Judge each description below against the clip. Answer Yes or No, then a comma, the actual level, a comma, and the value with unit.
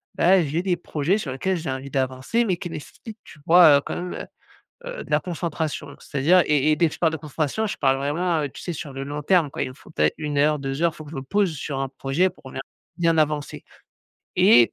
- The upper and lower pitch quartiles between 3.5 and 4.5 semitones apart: Yes, average, 3.9 semitones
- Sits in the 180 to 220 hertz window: No, medium, 150 Hz